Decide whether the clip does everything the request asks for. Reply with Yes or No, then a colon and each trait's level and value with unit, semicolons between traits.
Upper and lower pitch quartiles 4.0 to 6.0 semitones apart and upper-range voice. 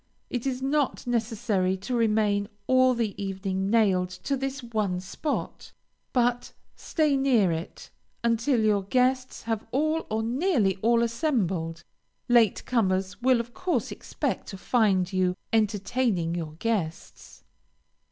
Yes: average, 4.7 semitones; high, 225 Hz